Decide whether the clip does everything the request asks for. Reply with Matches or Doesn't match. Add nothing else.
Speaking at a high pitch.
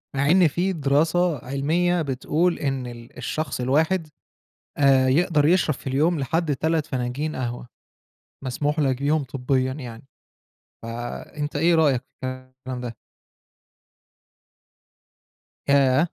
Doesn't match